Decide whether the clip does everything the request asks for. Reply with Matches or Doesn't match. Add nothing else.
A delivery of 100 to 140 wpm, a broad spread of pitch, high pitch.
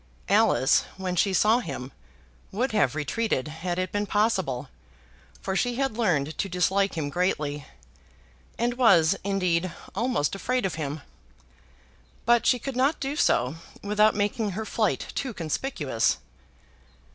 Matches